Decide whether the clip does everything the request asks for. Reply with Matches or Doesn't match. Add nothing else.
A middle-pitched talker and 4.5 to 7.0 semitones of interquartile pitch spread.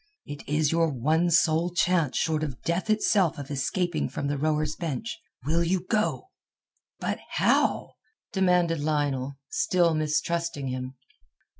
Doesn't match